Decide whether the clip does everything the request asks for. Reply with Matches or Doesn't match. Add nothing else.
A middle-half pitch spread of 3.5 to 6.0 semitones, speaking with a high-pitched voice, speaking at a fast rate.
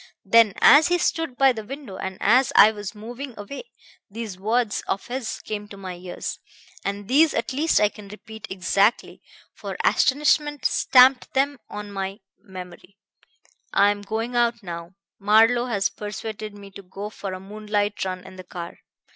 Doesn't match